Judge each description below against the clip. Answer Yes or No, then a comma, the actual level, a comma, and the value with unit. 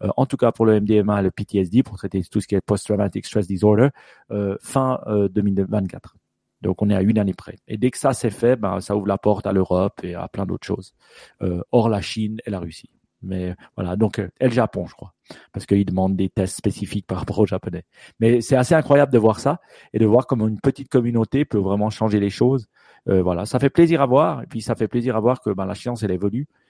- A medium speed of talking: No, fast, 250 wpm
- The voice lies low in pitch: Yes, low, 105 Hz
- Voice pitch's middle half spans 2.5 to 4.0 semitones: Yes, average, 3.6 semitones